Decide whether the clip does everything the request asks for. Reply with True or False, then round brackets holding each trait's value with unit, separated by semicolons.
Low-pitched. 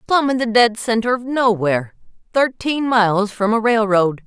False (225 Hz)